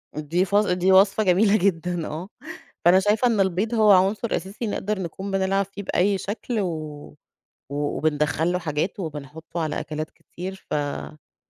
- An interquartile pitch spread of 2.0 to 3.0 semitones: No, average, 4.0 semitones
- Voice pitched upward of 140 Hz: Yes, medium, 185 Hz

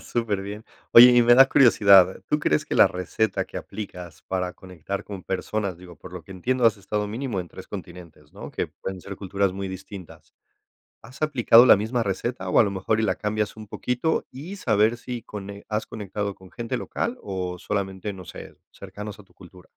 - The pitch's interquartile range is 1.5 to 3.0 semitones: No, average, 3.7 semitones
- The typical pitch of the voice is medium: No, low, 100 Hz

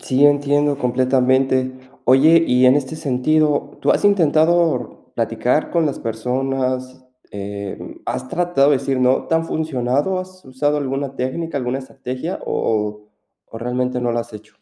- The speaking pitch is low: Yes, low, 130 Hz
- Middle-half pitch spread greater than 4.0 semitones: No, average, 2.9 semitones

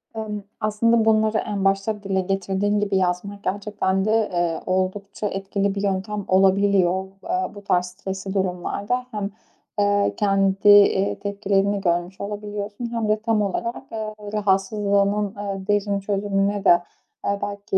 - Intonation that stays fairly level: Yes, narrow, 1.4 semitones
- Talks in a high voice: Yes, high, 200 Hz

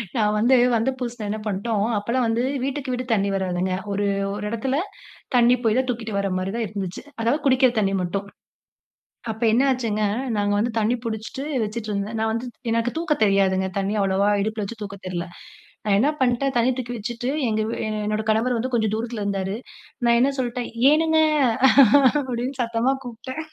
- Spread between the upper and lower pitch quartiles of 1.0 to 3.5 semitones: Yes, average, 3.2 semitones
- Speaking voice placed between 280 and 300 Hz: No, high, 225 Hz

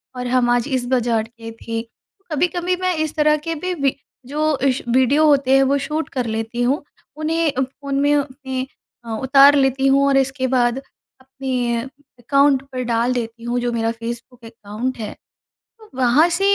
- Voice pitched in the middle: No, very high, 260 Hz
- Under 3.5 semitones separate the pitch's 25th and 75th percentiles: Yes, average, 3.0 semitones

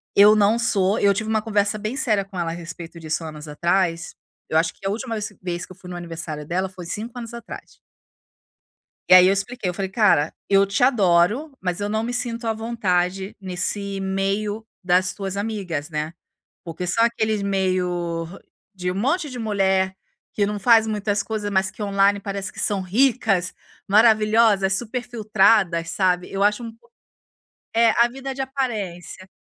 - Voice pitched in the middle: No, high, 200 Hz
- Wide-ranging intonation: No, average, 3.4 semitones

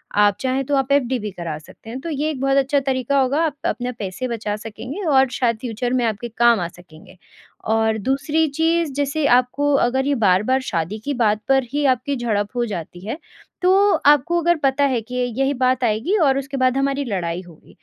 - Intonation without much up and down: No, average, 4.4 semitones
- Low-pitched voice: No, very high, 255 Hz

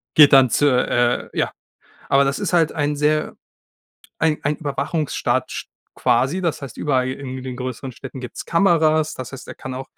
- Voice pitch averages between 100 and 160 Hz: Yes, medium, 140 Hz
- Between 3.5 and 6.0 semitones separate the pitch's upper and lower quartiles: No, average, 3.0 semitones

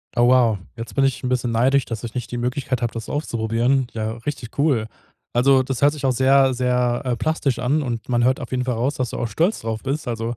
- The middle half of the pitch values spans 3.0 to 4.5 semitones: No, narrow, 2.4 semitones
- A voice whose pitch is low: Yes, low, 125 Hz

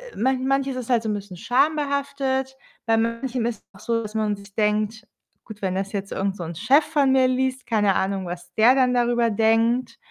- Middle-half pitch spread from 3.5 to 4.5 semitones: Yes, average, 4.2 semitones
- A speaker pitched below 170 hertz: No, high, 230 Hz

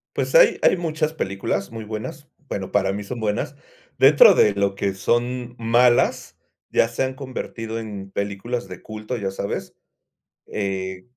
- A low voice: Yes, low, 110 Hz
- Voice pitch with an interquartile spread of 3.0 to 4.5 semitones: Yes, average, 4.0 semitones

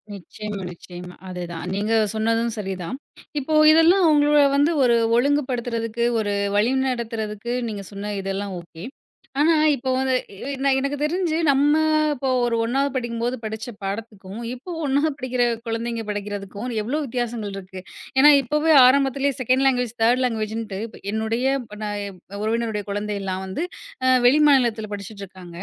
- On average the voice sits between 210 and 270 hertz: Yes, high, 230 Hz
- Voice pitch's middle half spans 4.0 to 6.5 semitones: Yes, average, 4.3 semitones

